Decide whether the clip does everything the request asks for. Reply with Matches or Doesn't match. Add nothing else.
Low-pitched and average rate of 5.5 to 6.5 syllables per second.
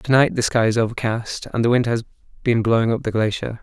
Matches